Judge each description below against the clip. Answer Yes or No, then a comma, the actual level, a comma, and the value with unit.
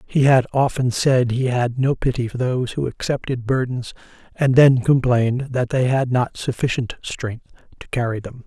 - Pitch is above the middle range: No, low, 125 Hz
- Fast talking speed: No, average, 175 wpm